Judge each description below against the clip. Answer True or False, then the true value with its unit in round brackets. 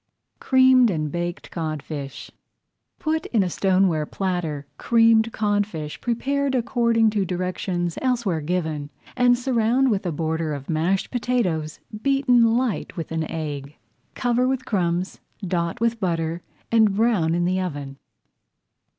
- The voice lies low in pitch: False (185 Hz)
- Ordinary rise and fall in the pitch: False (6.4 semitones)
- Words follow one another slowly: True (130 wpm)